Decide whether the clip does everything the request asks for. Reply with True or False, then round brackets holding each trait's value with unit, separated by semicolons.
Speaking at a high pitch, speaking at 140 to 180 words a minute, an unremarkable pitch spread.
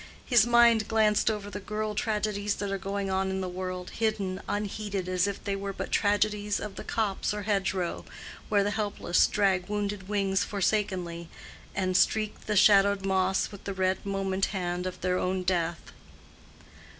False (200 Hz; 170 wpm; 1.9 semitones)